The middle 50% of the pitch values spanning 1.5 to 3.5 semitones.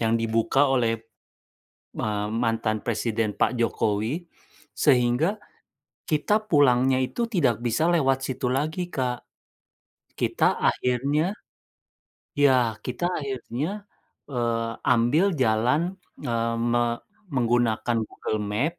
Yes: average, 3.0 semitones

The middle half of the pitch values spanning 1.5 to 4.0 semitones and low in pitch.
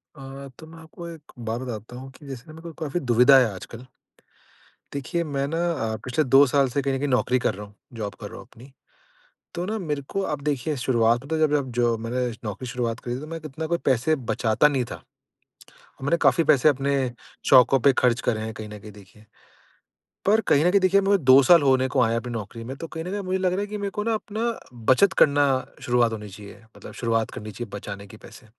No: average, 4.9 semitones; low, 130 Hz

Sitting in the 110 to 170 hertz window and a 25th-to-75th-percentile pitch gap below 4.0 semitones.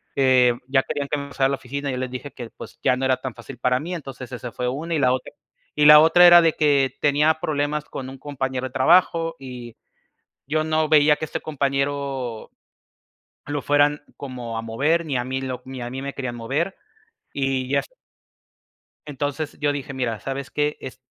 Yes: medium, 140 Hz; narrow, 2.5 semitones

